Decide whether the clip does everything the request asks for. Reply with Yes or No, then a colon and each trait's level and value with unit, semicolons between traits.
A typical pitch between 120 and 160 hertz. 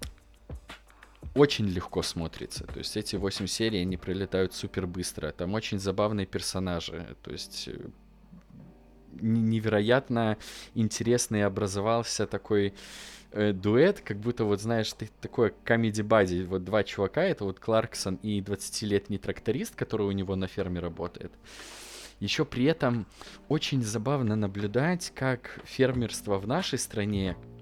No: low, 105 Hz